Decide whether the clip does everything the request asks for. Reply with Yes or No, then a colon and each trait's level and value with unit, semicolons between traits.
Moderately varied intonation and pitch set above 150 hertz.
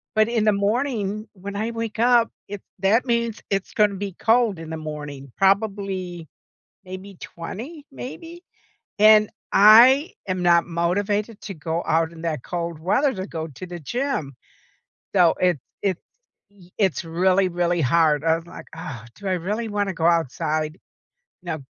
Yes: average, 4.3 semitones; high, 190 Hz